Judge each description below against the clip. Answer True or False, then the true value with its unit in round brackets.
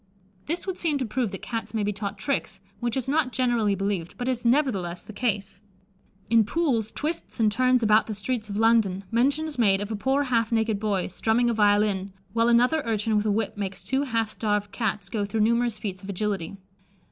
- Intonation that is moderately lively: True (3.2 semitones)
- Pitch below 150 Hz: False (220 Hz)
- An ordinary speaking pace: False (210 wpm)